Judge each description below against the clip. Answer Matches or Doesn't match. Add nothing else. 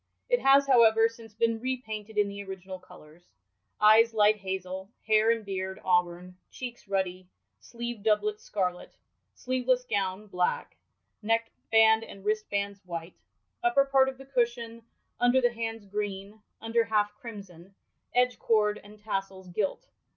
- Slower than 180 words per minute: Matches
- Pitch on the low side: Doesn't match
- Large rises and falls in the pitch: Doesn't match